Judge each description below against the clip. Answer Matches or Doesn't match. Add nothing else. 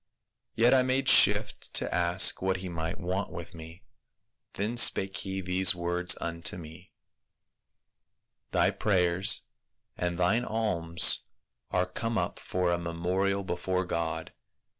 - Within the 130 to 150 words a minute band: Matches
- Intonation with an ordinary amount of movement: Doesn't match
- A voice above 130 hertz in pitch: Doesn't match